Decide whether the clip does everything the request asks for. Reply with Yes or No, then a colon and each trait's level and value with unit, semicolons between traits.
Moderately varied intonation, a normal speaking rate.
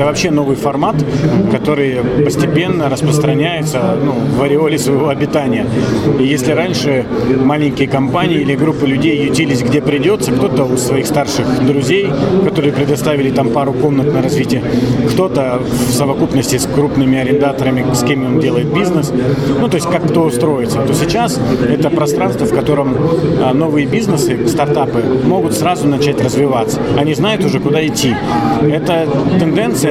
No: narrow, 2.2 semitones; average, 145 wpm